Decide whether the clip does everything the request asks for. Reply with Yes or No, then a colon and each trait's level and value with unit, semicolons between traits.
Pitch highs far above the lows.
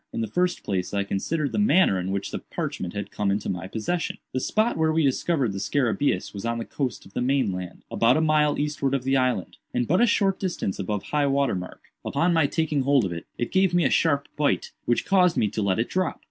Yes: wide, 7.8 semitones